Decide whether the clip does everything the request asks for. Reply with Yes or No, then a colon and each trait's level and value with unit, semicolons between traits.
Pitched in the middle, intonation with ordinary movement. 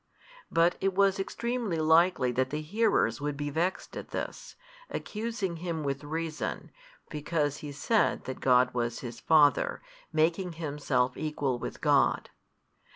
Yes: medium, 155 Hz; average, 4.4 semitones